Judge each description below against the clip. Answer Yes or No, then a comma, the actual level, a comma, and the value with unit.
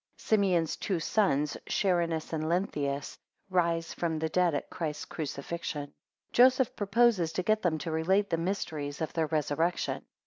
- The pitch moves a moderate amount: Yes, average, 3.4 semitones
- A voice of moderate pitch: Yes, medium, 165 Hz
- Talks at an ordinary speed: Yes, average, 160 wpm